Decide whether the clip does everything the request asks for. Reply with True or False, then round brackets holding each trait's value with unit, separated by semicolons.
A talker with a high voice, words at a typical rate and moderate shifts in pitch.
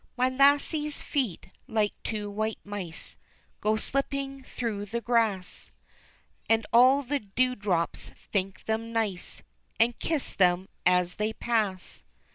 False (220 Hz; 125 wpm; 4.2 semitones)